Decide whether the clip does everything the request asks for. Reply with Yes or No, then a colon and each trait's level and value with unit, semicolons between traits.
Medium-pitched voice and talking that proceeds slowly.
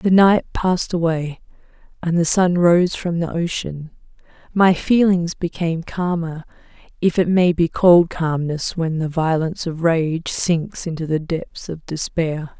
No: medium, 170 Hz; average, 150 wpm